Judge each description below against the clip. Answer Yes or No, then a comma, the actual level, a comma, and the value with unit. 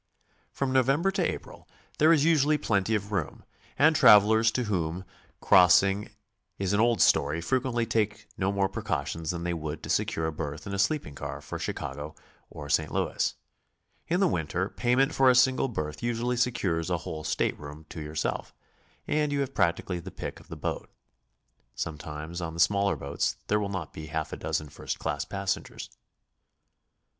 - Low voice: Yes, low, 100 Hz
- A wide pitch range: Yes, wide, 7.4 semitones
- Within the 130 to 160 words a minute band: No, average, 175 wpm